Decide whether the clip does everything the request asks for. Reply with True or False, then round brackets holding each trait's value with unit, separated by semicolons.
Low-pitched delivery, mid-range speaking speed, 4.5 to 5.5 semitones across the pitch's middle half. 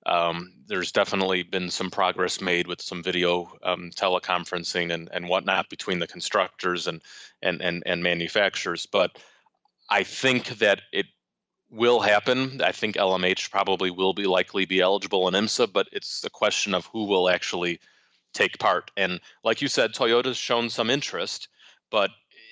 True (95 Hz; 160 wpm; 5.0 semitones)